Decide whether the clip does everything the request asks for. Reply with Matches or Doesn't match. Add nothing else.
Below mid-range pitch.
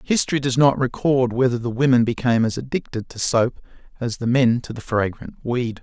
Matches